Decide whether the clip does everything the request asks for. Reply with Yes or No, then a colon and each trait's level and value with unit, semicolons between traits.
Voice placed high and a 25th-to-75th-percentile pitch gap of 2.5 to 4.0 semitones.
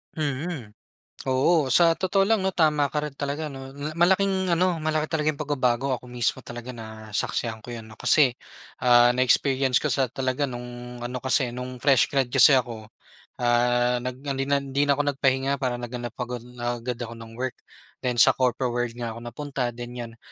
No: low, 130 Hz; average, 3.1 semitones